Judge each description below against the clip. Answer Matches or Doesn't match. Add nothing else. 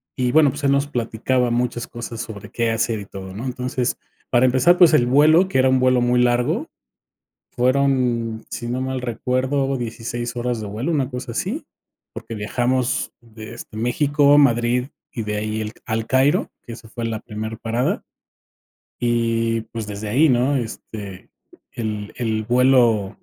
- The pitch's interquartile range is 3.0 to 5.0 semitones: Doesn't match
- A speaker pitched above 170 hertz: Doesn't match